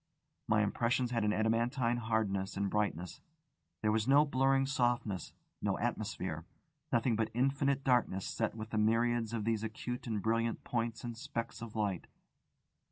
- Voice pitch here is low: Yes, low, 115 Hz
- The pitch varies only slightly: Yes, narrow, 2.2 semitones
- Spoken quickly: No, average, 155 wpm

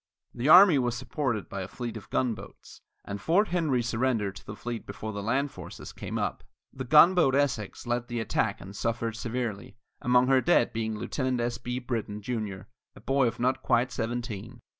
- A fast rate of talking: No, average, 185 wpm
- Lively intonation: No, average, 2.7 semitones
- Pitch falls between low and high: No, low, 120 Hz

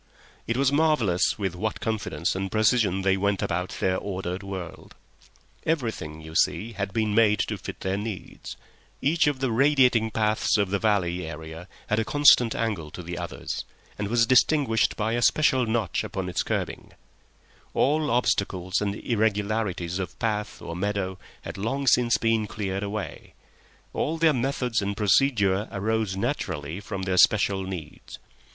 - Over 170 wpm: No, average, 160 wpm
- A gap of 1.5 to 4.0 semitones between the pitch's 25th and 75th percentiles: Yes, average, 3.6 semitones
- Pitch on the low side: Yes, low, 105 Hz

